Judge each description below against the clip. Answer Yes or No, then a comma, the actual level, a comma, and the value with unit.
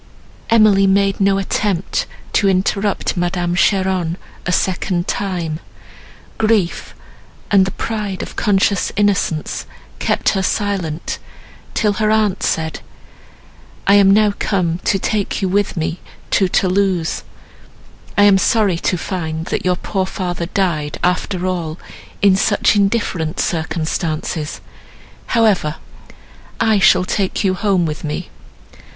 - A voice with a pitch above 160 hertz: Yes, high, 190 Hz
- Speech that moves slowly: Yes, slow, 125 wpm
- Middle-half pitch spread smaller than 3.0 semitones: Yes, narrow, 2.6 semitones